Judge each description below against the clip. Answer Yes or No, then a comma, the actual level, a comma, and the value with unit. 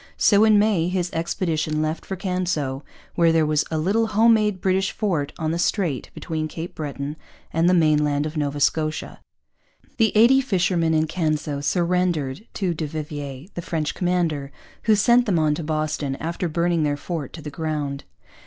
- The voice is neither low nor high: Yes, medium, 165 Hz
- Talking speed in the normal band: Yes, average, 175 wpm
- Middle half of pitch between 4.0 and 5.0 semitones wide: No, average, 3.3 semitones